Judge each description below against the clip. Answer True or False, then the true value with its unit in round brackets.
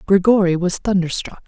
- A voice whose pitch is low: False (190 Hz)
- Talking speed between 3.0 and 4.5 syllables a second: False (5.3 syllables/s)